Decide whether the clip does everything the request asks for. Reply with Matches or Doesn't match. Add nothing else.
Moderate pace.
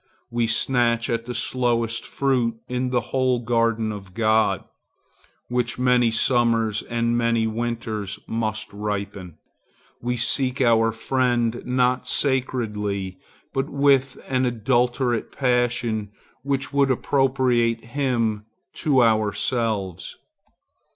Doesn't match